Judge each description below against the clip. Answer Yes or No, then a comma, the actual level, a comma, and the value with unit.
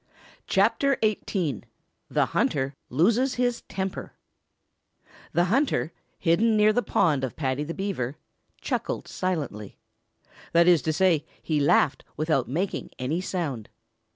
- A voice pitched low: No, medium, 170 Hz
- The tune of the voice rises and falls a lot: Yes, wide, 5.7 semitones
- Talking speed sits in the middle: No, slow, 125 wpm